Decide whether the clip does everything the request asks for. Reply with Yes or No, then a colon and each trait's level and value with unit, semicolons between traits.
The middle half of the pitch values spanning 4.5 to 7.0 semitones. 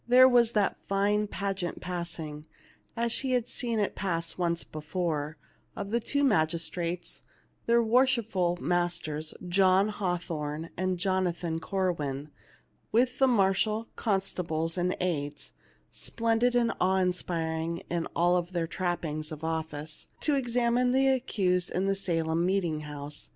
Yes: average, 4.9 semitones